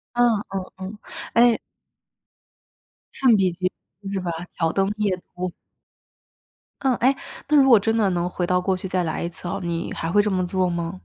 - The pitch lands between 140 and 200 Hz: Yes, medium, 185 Hz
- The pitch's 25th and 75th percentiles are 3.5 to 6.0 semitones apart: No, average, 3.1 semitones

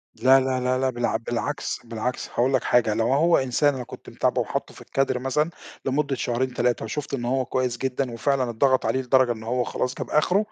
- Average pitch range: No, narrow, 1.9 semitones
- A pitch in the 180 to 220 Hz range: No, low, 130 Hz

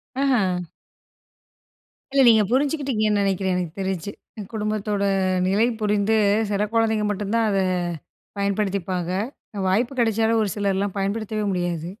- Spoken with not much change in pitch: Yes, narrow, 2.3 semitones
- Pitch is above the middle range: Yes, high, 205 Hz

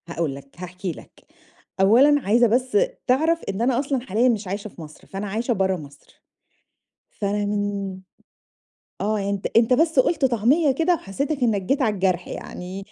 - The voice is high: Yes, high, 210 Hz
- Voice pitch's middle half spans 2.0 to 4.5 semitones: No, average, 5.2 semitones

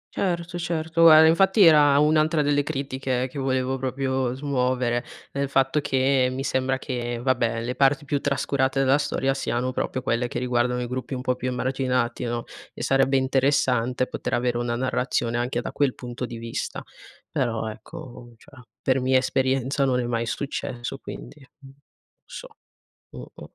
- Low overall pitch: Yes, low, 130 Hz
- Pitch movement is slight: Yes, narrow, 2.1 semitones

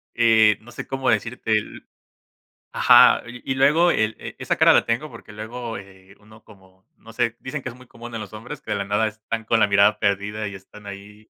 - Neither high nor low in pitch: No, low, 110 Hz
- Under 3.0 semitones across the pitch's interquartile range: Yes, narrow, 2.5 semitones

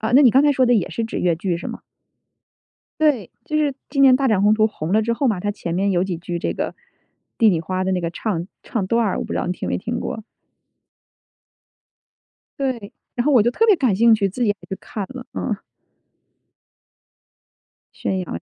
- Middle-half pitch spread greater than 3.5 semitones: Yes, average, 5.1 semitones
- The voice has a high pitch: Yes, high, 215 Hz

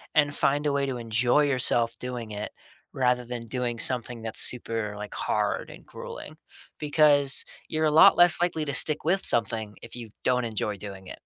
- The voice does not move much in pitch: No, average, 4.2 semitones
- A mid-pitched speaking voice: No, low, 125 Hz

